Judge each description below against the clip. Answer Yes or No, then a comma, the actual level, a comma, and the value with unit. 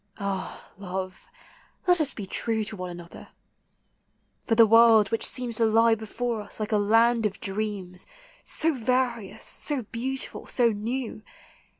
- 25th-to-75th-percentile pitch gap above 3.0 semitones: No, average, 2.7 semitones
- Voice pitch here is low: No, high, 225 Hz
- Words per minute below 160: Yes, average, 150 wpm